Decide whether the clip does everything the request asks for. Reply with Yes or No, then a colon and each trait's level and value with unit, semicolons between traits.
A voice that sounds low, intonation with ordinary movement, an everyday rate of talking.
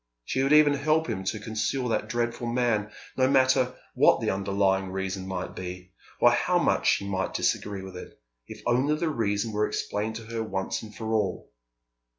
Yes: low, 110 Hz; average, 4.6 semitones; average, 185 wpm